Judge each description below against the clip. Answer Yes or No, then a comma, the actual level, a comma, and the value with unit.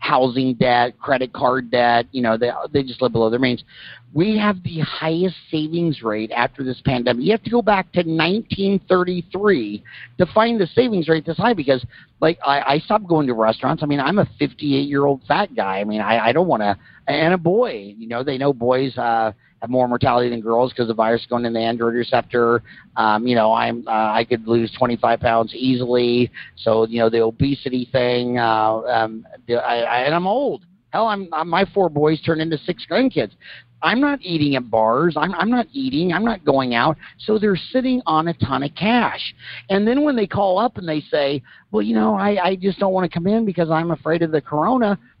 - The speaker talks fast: Yes, fast, 220 wpm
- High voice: No, medium, 140 Hz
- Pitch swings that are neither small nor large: No, wide, 7.2 semitones